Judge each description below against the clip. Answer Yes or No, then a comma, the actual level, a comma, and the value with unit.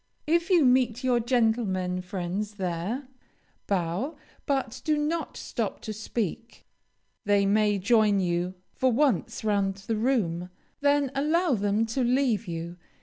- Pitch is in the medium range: No, high, 220 Hz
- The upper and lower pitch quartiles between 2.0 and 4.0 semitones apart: No, average, 5.3 semitones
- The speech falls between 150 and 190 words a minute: No, slow, 135 wpm